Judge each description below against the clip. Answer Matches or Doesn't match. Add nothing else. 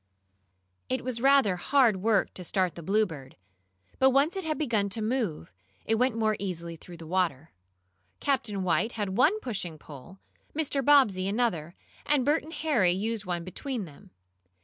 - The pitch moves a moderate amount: Doesn't match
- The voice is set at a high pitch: Matches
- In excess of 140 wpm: Matches